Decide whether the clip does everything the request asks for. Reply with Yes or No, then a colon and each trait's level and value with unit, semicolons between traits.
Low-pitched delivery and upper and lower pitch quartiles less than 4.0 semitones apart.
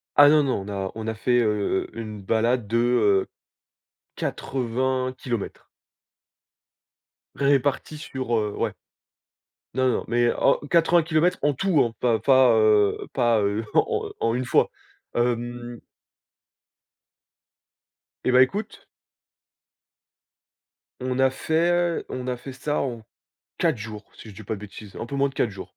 Yes: low, 120 Hz; average, 3.6 semitones